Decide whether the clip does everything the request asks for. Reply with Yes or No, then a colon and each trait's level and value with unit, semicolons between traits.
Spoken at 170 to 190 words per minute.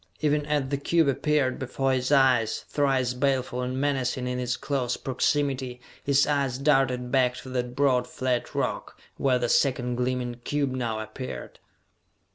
No: average, 155 wpm